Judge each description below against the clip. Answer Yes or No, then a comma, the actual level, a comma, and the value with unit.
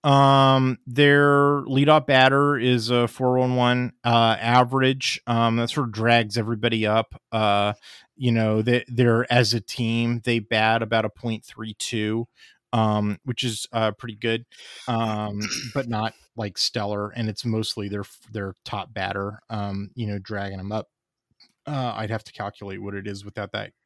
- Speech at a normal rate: Yes, average, 165 wpm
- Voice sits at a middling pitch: No, low, 115 Hz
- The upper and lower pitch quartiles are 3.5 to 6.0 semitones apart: No, average, 2.7 semitones